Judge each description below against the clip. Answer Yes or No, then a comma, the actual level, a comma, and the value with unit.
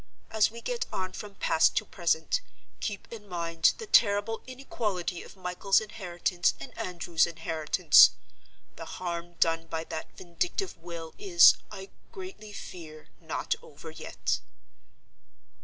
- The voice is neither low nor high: Yes, medium, 180 Hz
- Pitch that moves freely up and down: No, average, 3.9 semitones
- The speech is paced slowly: Yes, slow, 130 wpm